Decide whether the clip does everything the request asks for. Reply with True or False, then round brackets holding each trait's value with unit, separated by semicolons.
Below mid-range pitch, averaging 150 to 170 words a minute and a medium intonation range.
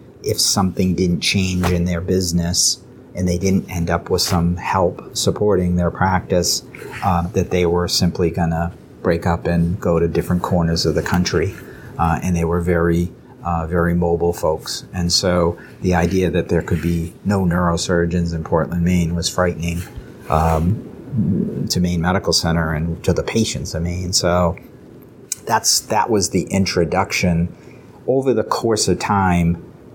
False (85 Hz; 160 wpm; 1.2 semitones)